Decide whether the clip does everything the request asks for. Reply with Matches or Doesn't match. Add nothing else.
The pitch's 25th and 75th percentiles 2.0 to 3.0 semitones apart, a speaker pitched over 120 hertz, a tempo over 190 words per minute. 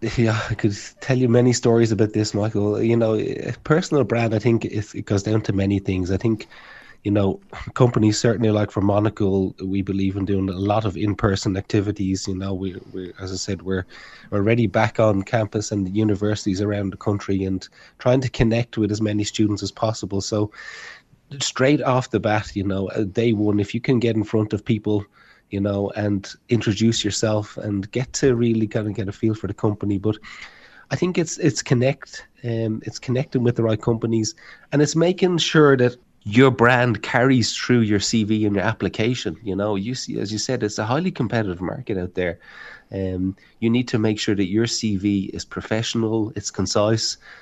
Doesn't match